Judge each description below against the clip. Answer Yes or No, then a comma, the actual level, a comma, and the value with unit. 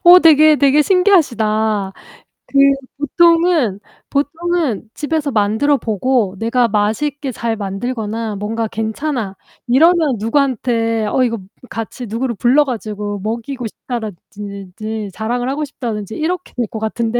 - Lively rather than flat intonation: No, average, 4.9 semitones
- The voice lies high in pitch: Yes, high, 235 Hz